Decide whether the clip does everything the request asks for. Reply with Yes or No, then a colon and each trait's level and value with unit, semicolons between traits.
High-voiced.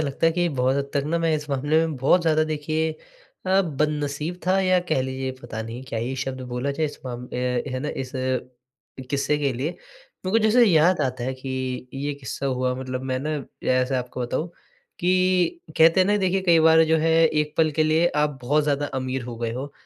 No: medium, 145 Hz